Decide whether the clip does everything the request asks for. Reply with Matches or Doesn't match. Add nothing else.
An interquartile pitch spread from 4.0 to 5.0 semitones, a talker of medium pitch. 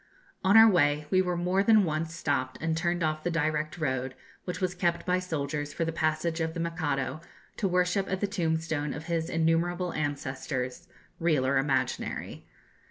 Doesn't match